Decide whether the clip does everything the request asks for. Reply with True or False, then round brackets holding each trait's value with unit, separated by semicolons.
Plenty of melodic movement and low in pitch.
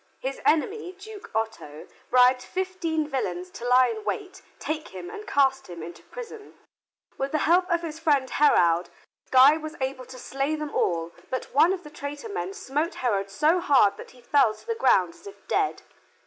False (6.0 semitones; 285 Hz)